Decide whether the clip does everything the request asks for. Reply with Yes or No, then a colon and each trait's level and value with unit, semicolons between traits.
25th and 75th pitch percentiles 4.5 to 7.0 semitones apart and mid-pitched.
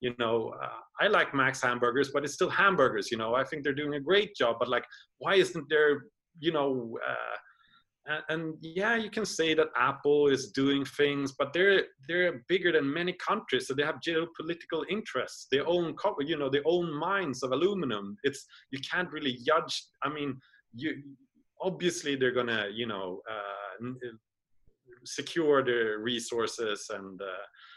Yes: average, 5.2 semitones; medium, 145 Hz